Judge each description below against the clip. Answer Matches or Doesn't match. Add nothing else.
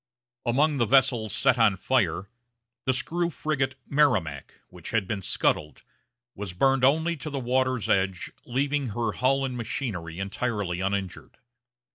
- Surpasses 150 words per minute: Doesn't match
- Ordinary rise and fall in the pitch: Doesn't match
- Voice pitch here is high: Doesn't match